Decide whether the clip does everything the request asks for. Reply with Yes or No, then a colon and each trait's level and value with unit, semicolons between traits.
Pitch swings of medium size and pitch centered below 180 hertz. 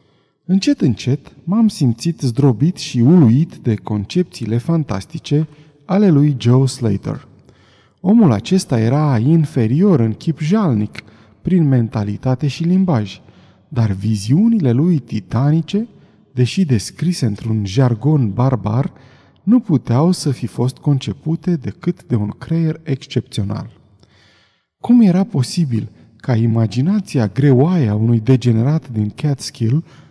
No: wide, 6.1 semitones; low, 135 Hz